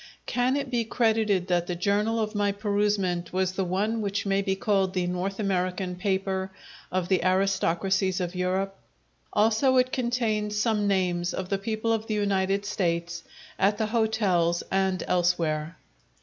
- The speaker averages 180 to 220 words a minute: No, average, 160 wpm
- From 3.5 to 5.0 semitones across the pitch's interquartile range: No, average, 2.7 semitones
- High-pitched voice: Yes, high, 195 Hz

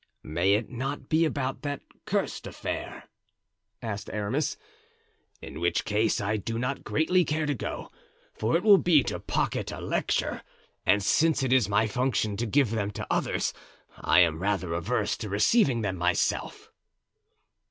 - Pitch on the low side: Yes, low, 115 Hz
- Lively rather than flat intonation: Yes, wide, 5.8 semitones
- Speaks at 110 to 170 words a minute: Yes, average, 160 wpm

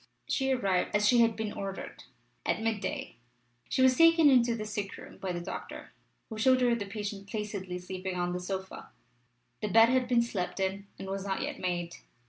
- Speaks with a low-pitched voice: No, high, 210 Hz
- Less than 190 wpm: No, average, 195 wpm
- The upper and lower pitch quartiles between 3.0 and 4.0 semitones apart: Yes, average, 3.7 semitones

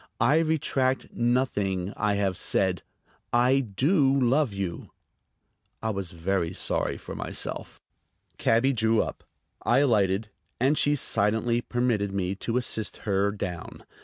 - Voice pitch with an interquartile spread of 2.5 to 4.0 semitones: No, average, 4.7 semitones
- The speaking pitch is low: Yes, low, 110 Hz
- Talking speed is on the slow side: Yes, slow, 130 wpm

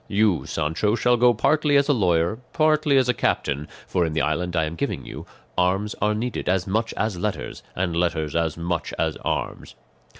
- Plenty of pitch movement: Yes, wide, 5.8 semitones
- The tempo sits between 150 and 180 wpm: No, average, 195 wpm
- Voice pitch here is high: No, very low, 95 Hz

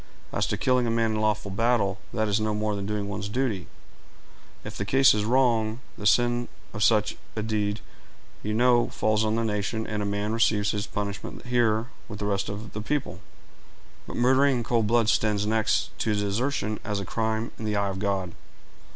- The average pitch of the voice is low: Yes, low, 110 Hz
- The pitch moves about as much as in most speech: No, narrow, 2.1 semitones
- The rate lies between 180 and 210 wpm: Yes, average, 200 wpm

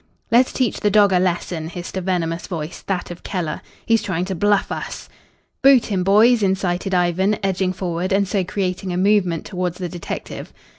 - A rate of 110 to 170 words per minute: No, average, 185 wpm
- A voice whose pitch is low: No, medium, 185 Hz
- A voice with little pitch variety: Yes, narrow, 2.2 semitones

